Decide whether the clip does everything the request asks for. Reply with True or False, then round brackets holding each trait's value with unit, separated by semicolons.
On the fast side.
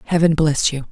False (195 wpm)